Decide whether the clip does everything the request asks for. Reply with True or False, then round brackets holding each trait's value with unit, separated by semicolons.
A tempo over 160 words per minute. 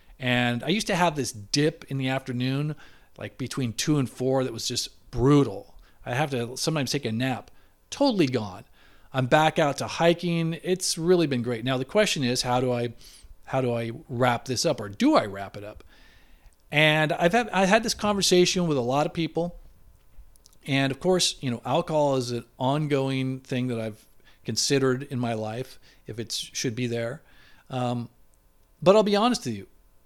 True (190 wpm)